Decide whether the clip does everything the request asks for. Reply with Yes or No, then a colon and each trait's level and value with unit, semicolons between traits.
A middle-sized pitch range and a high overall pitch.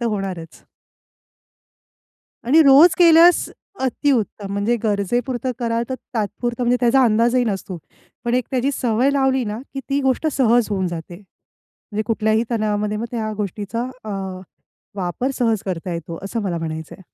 Yes: average, 4.0 semitones; high, 230 Hz